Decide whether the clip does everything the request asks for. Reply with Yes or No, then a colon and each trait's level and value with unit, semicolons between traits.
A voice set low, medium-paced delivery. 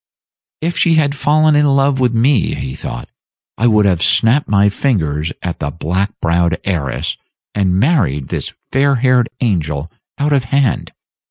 Yes: low, 115 Hz; average, 160 wpm